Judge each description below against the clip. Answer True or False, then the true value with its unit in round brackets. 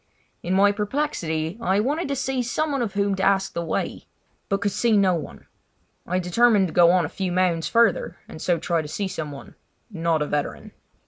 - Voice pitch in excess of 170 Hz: True (190 Hz)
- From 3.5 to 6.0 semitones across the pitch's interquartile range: True (4.5 semitones)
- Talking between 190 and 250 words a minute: True (195 wpm)